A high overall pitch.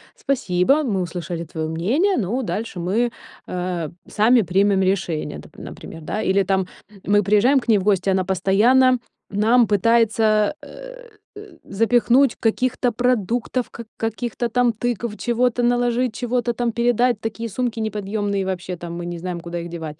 Yes: high, 215 Hz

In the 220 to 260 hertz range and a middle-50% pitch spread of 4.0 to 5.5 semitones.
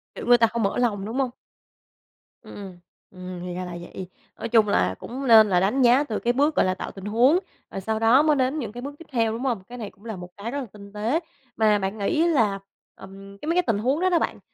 Yes: high, 225 Hz; average, 4.7 semitones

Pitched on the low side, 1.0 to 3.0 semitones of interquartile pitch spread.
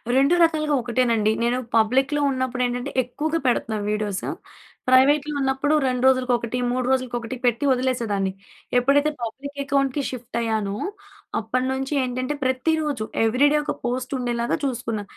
No: very high, 255 Hz; average, 2.7 semitones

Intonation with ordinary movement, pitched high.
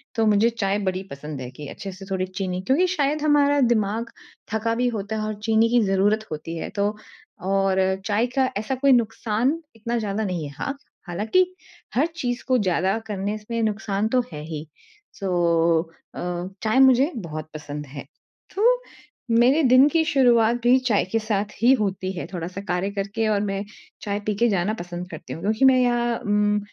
Yes: average, 4.2 semitones; high, 210 Hz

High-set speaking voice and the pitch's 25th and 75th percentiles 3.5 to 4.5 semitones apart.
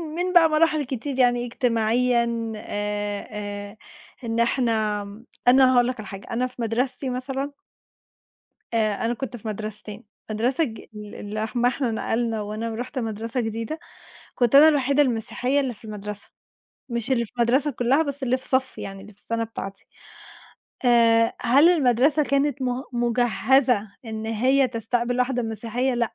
No: high, 240 Hz; average, 2.9 semitones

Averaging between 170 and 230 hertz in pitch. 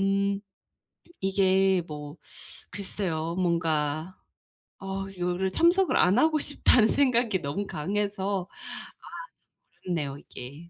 Yes: high, 190 Hz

